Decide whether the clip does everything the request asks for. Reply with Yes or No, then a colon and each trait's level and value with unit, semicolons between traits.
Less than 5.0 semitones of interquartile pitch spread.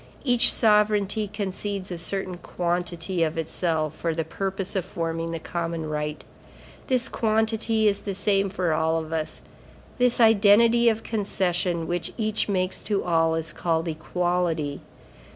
Yes: average, 4.1 semitones